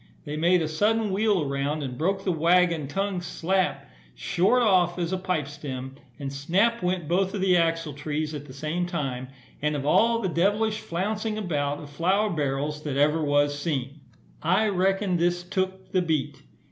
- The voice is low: No, medium, 170 Hz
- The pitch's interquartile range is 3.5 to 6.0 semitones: Yes, average, 4.5 semitones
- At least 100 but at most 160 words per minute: No, average, 170 wpm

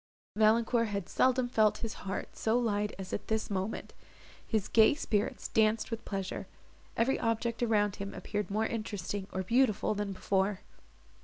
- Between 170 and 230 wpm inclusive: No, average, 155 wpm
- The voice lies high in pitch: Yes, high, 215 Hz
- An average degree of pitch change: No, narrow, 2.3 semitones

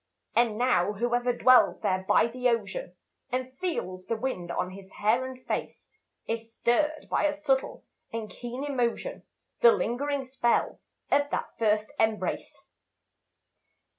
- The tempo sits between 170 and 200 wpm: No, slow, 135 wpm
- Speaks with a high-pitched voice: Yes, high, 240 Hz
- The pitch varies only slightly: No, average, 3.3 semitones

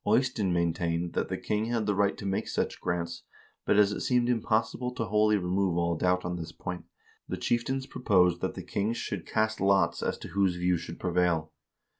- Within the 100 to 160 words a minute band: No, average, 200 wpm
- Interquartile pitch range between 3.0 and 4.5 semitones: Yes, average, 3.8 semitones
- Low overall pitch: Yes, very low, 95 Hz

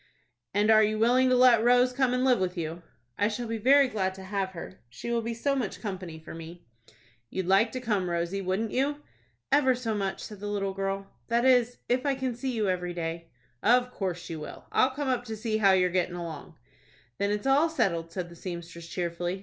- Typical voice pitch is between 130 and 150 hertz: No, high, 205 Hz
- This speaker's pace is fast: Yes, fast, 220 wpm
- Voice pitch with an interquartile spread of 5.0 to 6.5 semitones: Yes, wide, 5.4 semitones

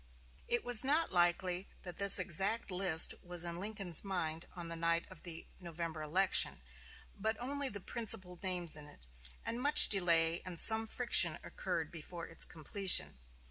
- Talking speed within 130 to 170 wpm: Yes, average, 160 wpm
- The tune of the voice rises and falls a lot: No, average, 3.9 semitones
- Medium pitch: Yes, medium, 180 Hz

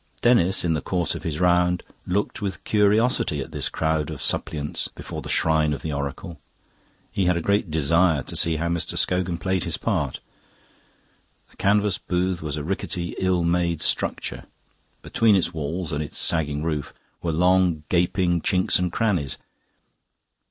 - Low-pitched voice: Yes, very low, 85 Hz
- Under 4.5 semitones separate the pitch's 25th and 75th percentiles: Yes, average, 3.0 semitones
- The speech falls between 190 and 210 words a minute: No, average, 165 wpm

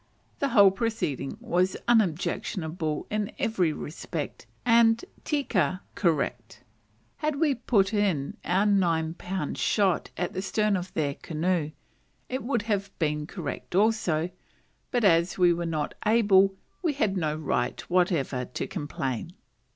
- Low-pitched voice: No, medium, 185 Hz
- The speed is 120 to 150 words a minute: Yes, slow, 135 wpm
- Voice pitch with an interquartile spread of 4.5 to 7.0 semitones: Yes, average, 5.1 semitones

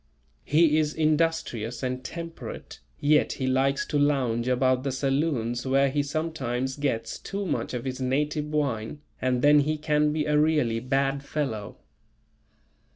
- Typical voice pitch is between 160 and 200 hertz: No, medium, 140 Hz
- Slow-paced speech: No, average, 150 wpm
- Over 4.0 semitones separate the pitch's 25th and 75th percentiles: No, average, 2.8 semitones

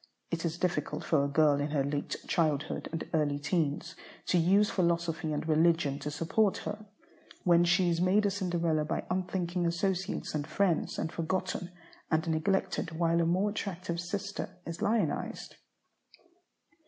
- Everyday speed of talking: Yes, average, 155 wpm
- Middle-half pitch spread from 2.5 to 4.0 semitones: Yes, average, 2.8 semitones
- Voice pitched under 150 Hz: No, medium, 170 Hz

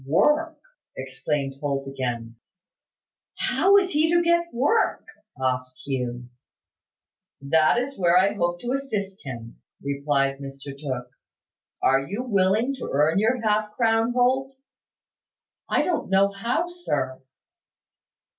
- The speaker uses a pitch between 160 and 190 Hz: Yes, medium, 185 Hz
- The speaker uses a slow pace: Yes, slow, 120 wpm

